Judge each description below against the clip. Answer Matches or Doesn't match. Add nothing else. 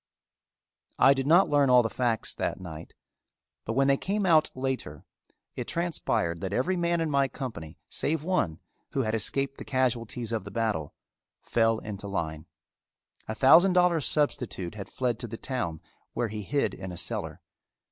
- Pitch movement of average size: Doesn't match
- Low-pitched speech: Matches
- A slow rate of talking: Doesn't match